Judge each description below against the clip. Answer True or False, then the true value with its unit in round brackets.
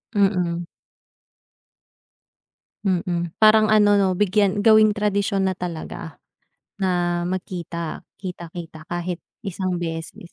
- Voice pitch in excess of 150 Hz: True (185 Hz)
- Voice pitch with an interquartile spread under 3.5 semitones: True (2.8 semitones)